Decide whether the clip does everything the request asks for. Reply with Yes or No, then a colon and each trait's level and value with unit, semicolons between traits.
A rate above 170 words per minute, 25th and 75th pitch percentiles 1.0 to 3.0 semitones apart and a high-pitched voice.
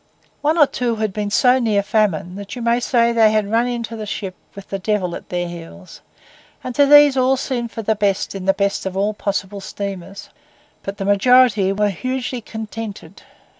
No: average, 195 wpm; average, 3.5 semitones; high, 210 Hz